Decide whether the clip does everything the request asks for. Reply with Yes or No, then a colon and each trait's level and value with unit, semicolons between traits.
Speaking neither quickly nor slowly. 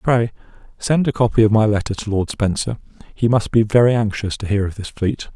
No: fast, 225 wpm